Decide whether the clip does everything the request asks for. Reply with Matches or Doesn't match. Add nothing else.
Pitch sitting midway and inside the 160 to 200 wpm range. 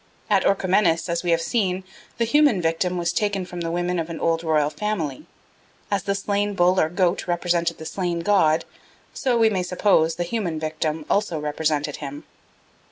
Matches